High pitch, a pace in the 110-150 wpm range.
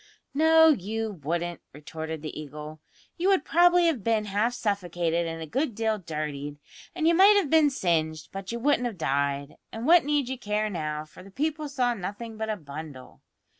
No: high, 205 Hz; average, 190 wpm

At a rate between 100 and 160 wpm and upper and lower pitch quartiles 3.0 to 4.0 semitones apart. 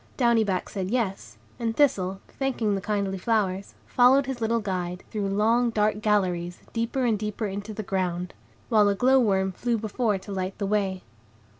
No: average, 175 wpm; average, 3.3 semitones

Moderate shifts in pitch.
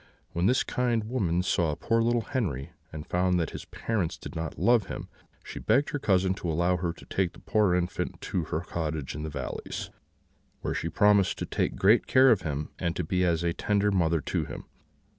Yes: average, 4.2 semitones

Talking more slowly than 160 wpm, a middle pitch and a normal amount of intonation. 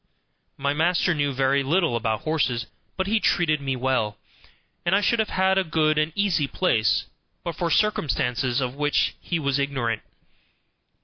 No: average, 165 wpm; medium, 145 Hz; average, 4.9 semitones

